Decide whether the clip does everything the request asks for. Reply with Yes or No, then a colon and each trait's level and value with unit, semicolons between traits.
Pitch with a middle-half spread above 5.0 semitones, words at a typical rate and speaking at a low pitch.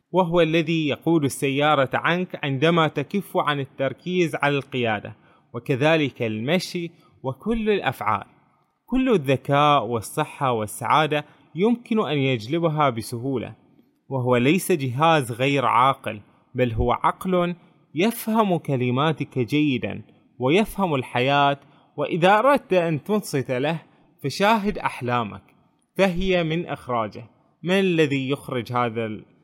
No: wide, 5.4 semitones; average, 100 wpm; medium, 150 Hz